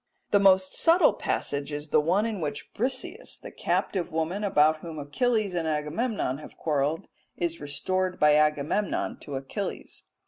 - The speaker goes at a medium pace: Yes, average, 150 wpm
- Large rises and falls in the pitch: No, average, 4.9 semitones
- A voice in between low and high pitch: Yes, medium, 160 Hz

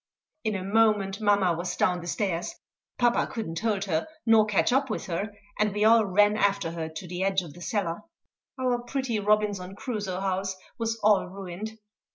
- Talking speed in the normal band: Yes, average, 190 wpm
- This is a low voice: No, high, 200 Hz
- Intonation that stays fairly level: No, average, 3.0 semitones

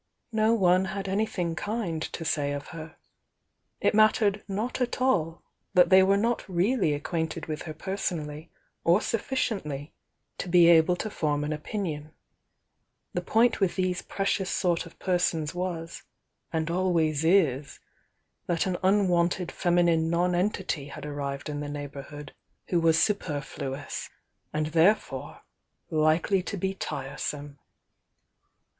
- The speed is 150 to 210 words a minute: No, average, 140 wpm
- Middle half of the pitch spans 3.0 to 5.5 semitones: Yes, average, 3.8 semitones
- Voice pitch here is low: No, medium, 170 Hz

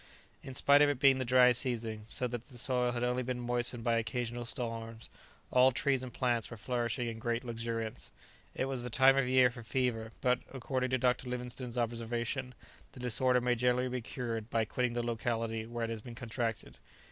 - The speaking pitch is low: Yes, low, 120 Hz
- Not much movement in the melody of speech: Yes, narrow, 1.6 semitones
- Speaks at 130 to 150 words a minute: No, average, 200 wpm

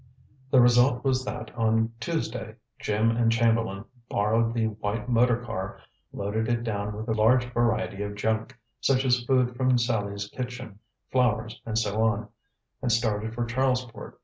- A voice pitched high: No, low, 115 Hz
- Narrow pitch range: Yes, narrow, 2.2 semitones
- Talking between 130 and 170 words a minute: Yes, average, 155 wpm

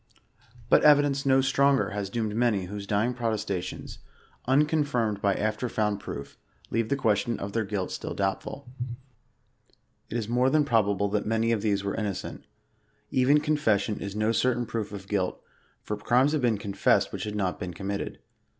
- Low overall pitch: Yes, low, 110 Hz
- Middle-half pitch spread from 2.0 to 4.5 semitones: Yes, average, 3.8 semitones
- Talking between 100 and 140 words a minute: No, average, 170 wpm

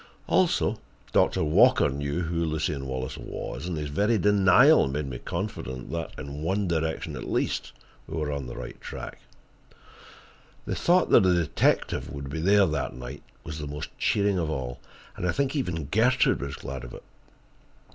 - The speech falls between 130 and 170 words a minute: No, average, 180 wpm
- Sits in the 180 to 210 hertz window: No, very low, 80 Hz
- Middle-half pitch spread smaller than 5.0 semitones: No, average, 5.3 semitones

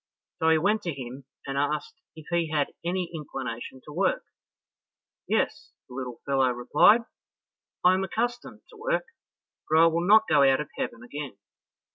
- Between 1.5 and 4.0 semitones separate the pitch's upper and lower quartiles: No, average, 5.2 semitones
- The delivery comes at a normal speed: Yes, average, 165 wpm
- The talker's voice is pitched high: No, medium, 155 Hz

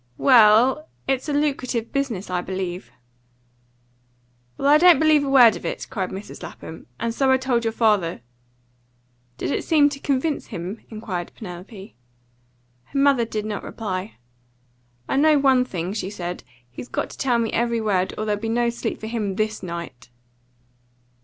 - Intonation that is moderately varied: No, wide, 5.8 semitones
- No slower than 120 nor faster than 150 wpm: No, average, 165 wpm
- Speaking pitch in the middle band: No, high, 225 Hz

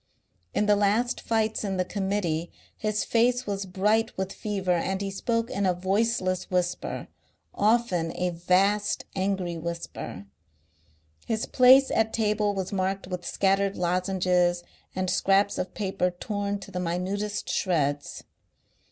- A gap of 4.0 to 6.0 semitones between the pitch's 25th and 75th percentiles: No, narrow, 2.5 semitones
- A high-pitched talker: Yes, high, 195 Hz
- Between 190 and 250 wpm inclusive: No, slow, 135 wpm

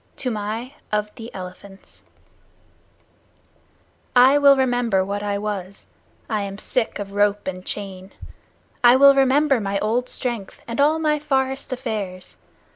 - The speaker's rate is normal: No, slow, 130 wpm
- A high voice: Yes, high, 220 Hz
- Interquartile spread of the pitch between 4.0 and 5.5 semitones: Yes, average, 4.6 semitones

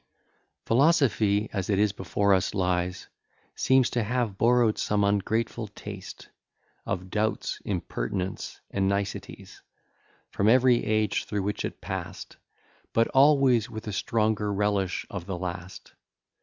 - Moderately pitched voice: No, low, 105 Hz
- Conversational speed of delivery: No, slow, 130 wpm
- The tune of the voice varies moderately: Yes, average, 3.1 semitones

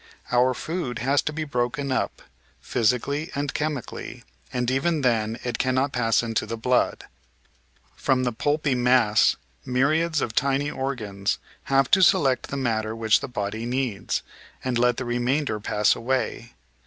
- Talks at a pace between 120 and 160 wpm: Yes, average, 150 wpm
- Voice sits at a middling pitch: No, low, 125 Hz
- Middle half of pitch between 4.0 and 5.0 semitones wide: No, average, 3.1 semitones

